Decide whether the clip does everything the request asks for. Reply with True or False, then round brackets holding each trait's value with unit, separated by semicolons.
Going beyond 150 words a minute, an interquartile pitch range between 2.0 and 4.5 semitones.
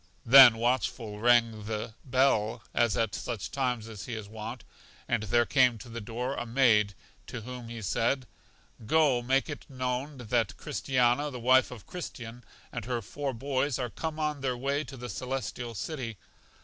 True (170 wpm; 2.8 semitones)